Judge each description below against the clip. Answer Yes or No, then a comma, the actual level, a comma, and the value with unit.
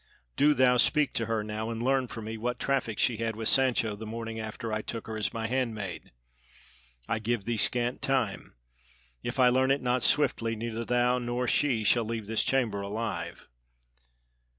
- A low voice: Yes, low, 115 Hz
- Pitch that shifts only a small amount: Yes, narrow, 2.2 semitones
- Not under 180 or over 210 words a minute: Yes, average, 185 wpm